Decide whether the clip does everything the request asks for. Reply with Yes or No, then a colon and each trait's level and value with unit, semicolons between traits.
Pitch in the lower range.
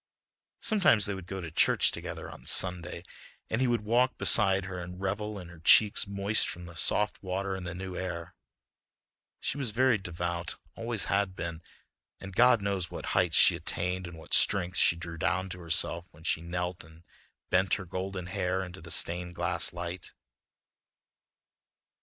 Yes: very low, 90 Hz